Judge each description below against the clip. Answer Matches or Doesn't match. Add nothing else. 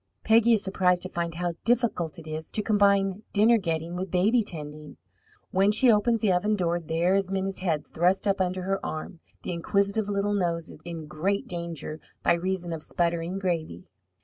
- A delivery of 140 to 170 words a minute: Doesn't match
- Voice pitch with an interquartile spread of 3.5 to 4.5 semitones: Doesn't match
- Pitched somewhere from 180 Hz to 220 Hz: Matches